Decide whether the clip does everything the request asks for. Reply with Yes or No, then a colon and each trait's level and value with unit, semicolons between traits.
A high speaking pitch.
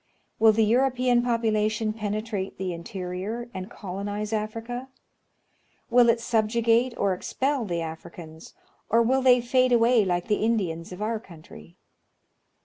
Yes: high, 220 Hz